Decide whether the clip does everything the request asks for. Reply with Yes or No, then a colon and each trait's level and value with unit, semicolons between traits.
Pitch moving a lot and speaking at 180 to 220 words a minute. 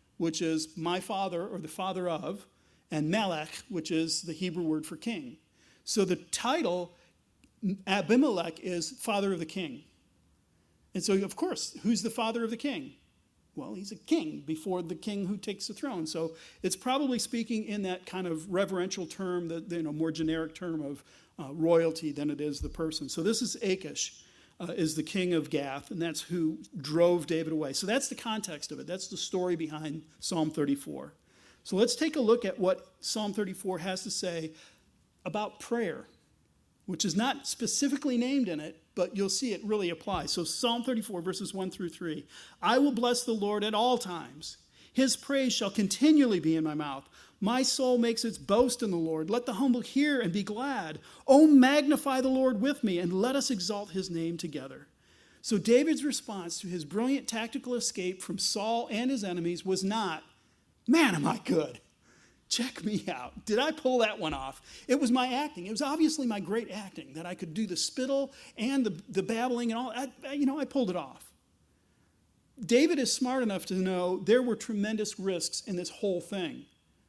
Yes: wide, 6.0 semitones; average, 195 wpm